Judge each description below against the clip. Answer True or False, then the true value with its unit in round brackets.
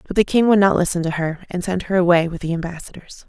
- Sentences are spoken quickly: True (275 wpm)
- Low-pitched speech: False (180 Hz)